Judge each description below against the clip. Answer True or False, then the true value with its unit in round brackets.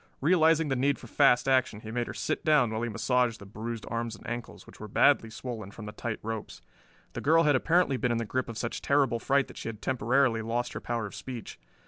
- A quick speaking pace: True (245 wpm)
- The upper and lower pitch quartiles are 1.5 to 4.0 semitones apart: True (3.1 semitones)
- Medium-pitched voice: False (120 Hz)